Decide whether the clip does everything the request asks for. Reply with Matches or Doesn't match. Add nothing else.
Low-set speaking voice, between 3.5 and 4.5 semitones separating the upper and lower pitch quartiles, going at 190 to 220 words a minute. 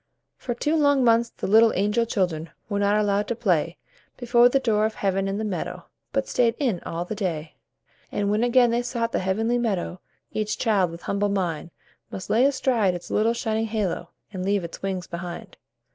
Doesn't match